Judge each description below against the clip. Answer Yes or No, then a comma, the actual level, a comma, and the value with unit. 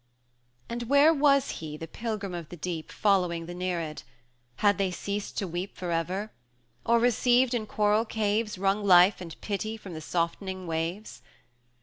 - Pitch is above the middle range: Yes, high, 195 Hz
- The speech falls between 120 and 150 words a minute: No, average, 165 wpm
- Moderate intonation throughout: Yes, average, 3.9 semitones